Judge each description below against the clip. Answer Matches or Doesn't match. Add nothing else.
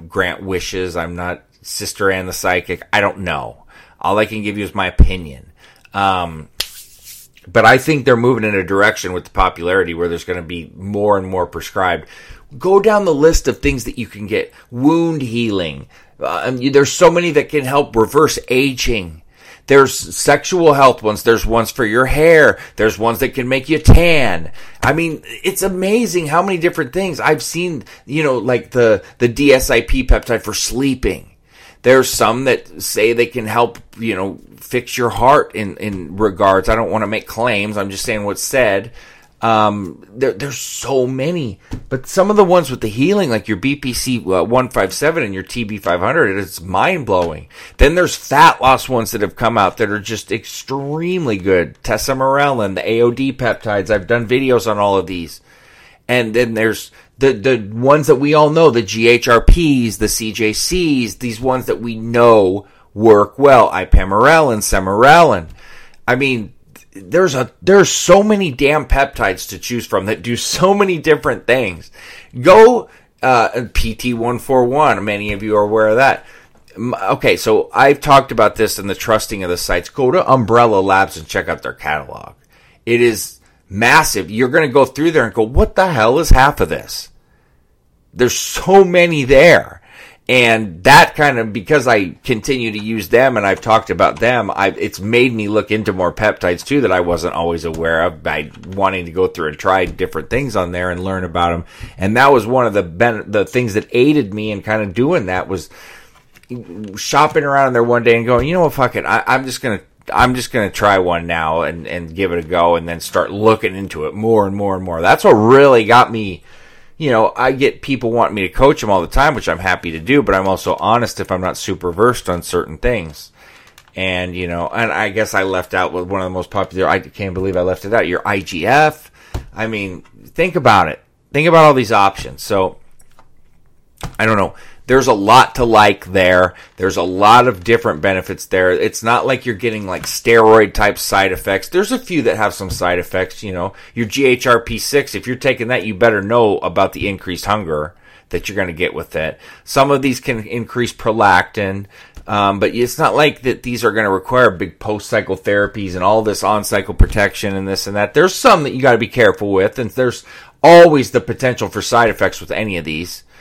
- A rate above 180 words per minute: Matches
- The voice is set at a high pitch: Doesn't match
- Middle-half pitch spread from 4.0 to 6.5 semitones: Matches